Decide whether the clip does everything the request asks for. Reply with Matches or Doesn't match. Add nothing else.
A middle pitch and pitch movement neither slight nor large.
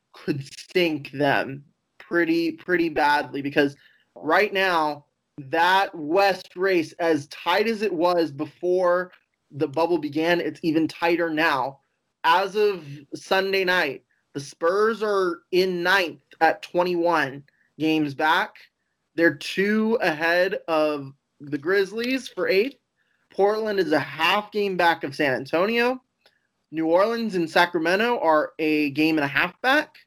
Matches